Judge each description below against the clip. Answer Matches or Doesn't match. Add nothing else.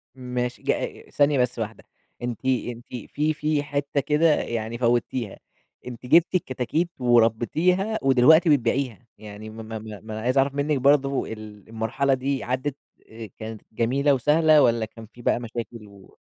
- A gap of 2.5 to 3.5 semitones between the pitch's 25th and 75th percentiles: Doesn't match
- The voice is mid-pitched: Doesn't match